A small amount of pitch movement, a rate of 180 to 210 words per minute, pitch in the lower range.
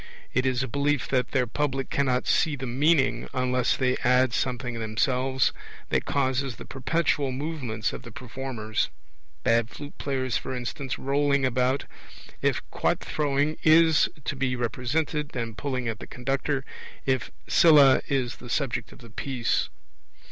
No: narrow, 2.2 semitones; average, 150 wpm; low, 130 Hz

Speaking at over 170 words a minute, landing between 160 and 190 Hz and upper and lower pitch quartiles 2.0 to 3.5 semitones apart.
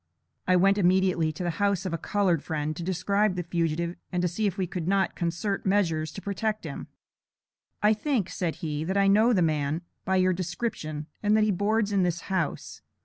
Yes: average, 200 wpm; medium, 185 Hz; average, 3.1 semitones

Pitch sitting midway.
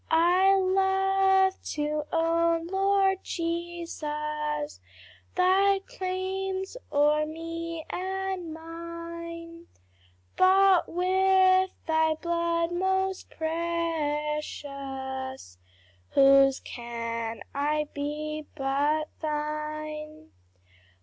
No: very high, 330 Hz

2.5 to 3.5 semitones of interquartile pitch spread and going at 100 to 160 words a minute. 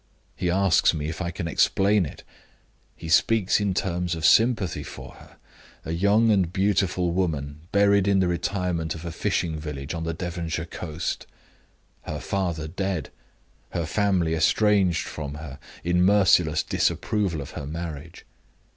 Yes: average, 3.2 semitones; average, 150 wpm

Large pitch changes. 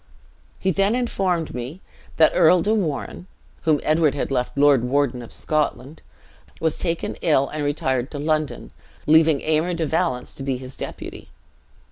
No: average, 3.3 semitones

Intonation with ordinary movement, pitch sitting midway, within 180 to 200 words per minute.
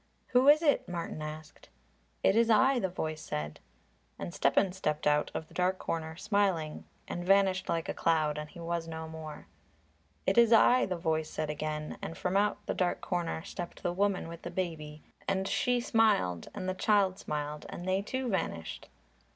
Yes: average, 4.2 semitones; medium, 175 Hz; average, 185 wpm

